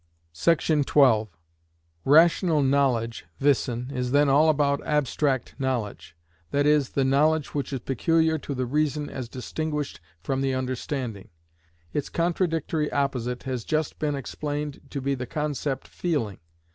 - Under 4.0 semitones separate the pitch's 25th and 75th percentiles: Yes, average, 2.9 semitones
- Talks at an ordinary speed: No, slow, 130 wpm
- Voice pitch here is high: No, medium, 140 Hz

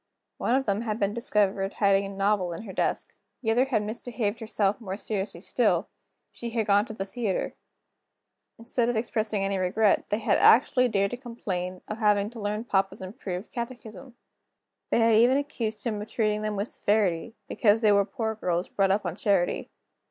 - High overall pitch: Yes, high, 210 Hz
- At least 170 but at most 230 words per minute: Yes, average, 190 wpm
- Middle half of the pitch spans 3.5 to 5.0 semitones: No, average, 2.8 semitones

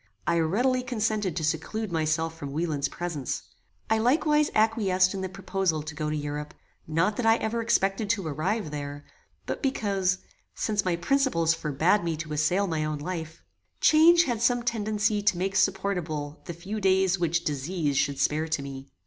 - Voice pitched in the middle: Yes, medium, 180 Hz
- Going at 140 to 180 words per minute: Yes, average, 175 wpm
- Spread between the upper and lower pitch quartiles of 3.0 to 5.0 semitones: No, wide, 5.6 semitones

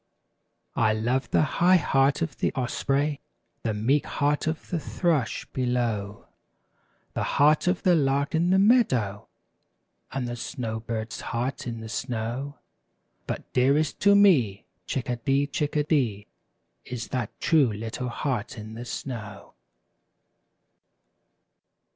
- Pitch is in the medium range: No, low, 130 Hz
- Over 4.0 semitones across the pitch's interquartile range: Yes, average, 4.6 semitones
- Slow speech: Yes, slow, 125 wpm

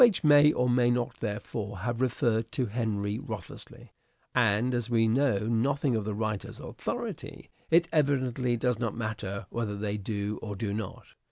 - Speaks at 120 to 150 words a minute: No, average, 160 wpm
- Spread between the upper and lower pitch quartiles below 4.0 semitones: Yes, average, 3.1 semitones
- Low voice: Yes, low, 115 Hz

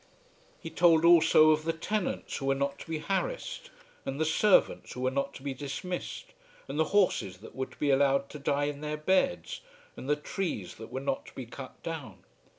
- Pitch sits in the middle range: Yes, medium, 150 Hz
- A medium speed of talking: No, fast, 210 wpm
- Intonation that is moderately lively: Yes, average, 3.6 semitones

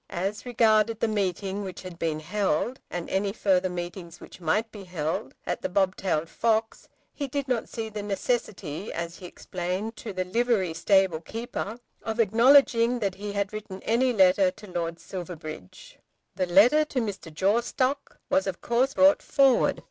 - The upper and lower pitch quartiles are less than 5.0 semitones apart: Yes, average, 4.1 semitones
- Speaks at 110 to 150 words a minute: No, average, 165 wpm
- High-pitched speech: Yes, high, 200 Hz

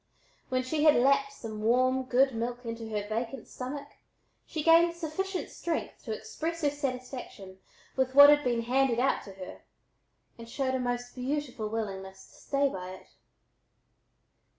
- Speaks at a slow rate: No, average, 155 wpm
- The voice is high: Yes, very high, 255 Hz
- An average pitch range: Yes, average, 3.9 semitones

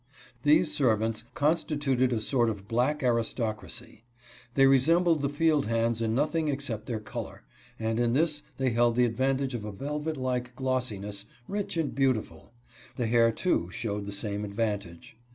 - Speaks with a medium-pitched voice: No, low, 120 Hz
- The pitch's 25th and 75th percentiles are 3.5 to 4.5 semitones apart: Yes, average, 4.2 semitones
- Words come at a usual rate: Yes, average, 155 wpm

